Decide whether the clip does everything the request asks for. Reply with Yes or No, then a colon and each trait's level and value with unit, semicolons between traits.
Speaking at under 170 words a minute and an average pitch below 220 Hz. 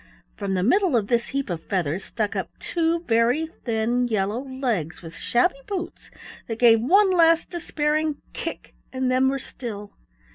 No: average, 160 wpm; very high, 250 Hz